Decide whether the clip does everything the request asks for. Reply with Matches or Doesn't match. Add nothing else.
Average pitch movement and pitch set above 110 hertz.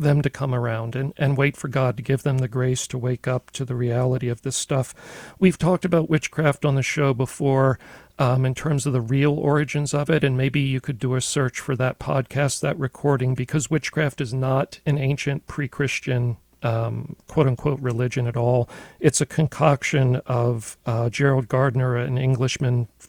Doesn't match